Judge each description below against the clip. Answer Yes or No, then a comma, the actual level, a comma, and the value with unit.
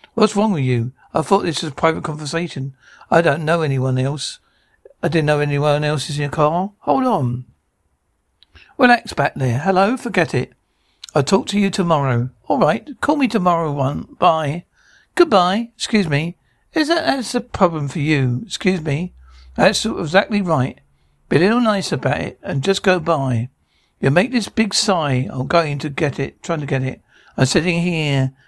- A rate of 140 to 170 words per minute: No, average, 185 wpm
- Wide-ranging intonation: Yes, wide, 6.5 semitones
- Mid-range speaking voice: Yes, medium, 160 Hz